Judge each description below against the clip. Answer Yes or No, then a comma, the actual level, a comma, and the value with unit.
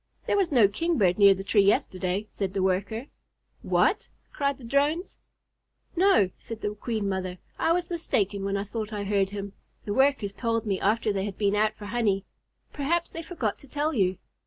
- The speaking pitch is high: Yes, high, 210 Hz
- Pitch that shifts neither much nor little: No, wide, 5.9 semitones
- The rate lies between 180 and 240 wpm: Yes, average, 190 wpm